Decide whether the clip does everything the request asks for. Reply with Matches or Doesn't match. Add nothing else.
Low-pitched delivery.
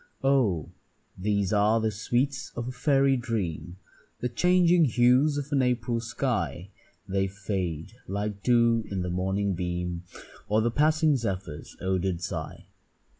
Matches